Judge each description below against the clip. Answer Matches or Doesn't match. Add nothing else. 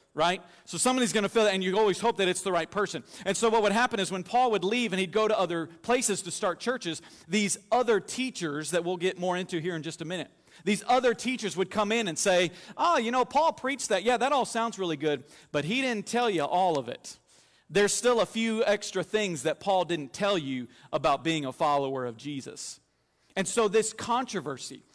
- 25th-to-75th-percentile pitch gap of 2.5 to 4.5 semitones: Doesn't match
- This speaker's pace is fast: Matches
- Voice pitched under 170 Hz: Doesn't match